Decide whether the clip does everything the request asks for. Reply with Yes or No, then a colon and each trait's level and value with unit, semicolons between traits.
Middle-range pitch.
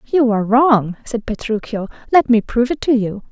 No: high, 230 Hz